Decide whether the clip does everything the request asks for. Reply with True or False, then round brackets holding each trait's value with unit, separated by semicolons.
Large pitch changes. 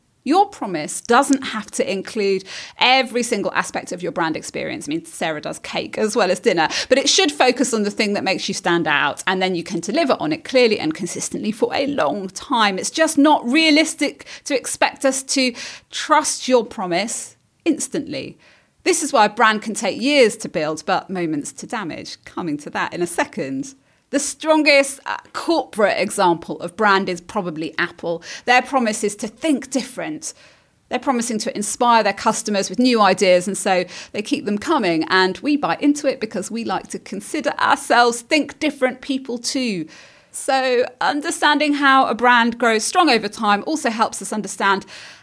True (5.9 semitones)